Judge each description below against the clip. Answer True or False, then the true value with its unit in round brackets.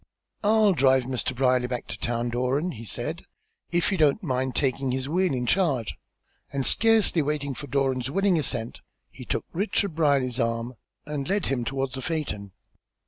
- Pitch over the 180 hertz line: False (135 Hz)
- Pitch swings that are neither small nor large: True (4.5 semitones)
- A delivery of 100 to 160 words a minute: False (170 wpm)